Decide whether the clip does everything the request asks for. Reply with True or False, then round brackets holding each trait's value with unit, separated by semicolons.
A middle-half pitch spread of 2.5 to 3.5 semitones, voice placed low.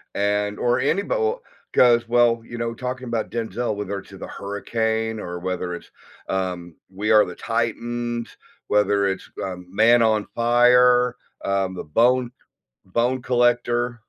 True (3.2 semitones; 115 Hz)